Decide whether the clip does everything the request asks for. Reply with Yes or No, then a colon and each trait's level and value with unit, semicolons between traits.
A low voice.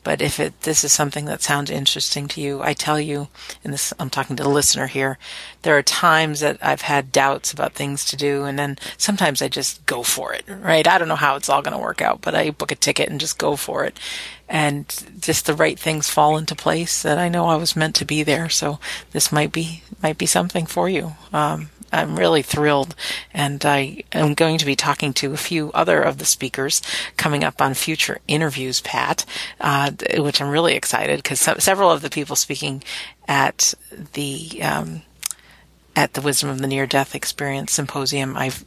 No: medium, 145 Hz